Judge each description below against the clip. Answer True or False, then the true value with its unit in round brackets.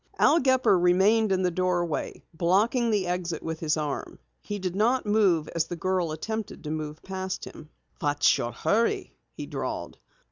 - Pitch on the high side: False (180 Hz)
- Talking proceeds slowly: False (170 wpm)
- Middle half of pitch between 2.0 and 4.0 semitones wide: False (4.4 semitones)